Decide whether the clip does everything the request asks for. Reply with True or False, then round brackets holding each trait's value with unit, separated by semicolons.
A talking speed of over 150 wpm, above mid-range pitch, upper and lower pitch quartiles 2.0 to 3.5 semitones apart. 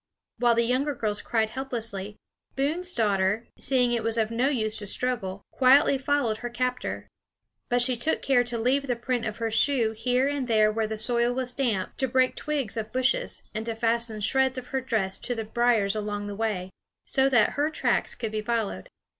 True (200 wpm; 235 Hz; 3.0 semitones)